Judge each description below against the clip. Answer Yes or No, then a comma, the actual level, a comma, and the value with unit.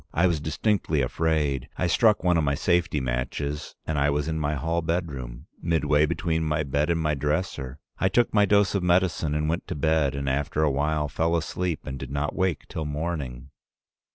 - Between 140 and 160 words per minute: No, average, 200 wpm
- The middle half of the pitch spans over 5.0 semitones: No, average, 3.0 semitones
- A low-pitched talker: Yes, very low, 75 Hz